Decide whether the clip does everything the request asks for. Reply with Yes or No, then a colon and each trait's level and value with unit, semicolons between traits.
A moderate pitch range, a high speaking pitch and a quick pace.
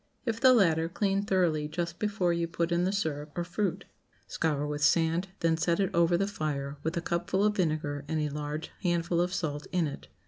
No: average, 3.0 semitones; medium, 170 Hz; fast, 210 wpm